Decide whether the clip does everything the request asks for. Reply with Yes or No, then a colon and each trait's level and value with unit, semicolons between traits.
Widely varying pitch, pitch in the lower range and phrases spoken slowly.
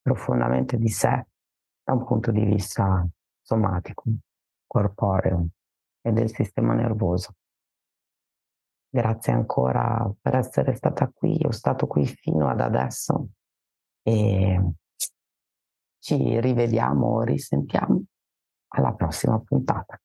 Yes: wide, 8.1 semitones; very low, 95 Hz; slow, 100 wpm